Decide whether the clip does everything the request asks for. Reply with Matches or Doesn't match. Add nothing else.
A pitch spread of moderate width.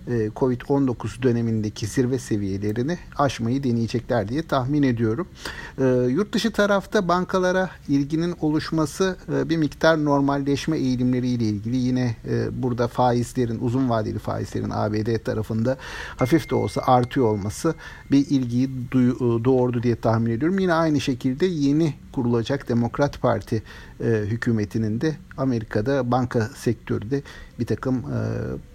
Matches